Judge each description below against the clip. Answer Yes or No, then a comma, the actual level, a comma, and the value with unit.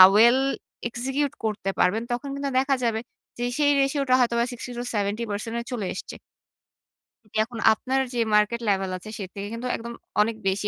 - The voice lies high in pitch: Yes, high, 235 Hz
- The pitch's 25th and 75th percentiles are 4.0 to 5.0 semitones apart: No, average, 2.9 semitones